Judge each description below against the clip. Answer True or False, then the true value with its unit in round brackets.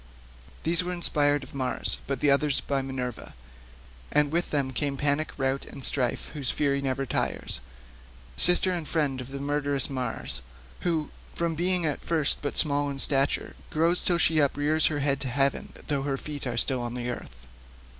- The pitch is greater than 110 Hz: True (140 Hz)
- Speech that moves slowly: False (170 wpm)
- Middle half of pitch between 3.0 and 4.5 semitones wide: False (2.5 semitones)